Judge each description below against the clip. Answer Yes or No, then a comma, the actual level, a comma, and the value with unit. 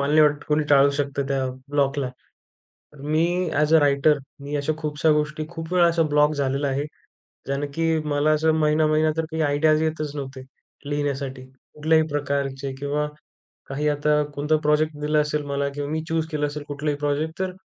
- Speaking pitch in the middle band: Yes, medium, 150 Hz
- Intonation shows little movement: Yes, narrow, 1.6 semitones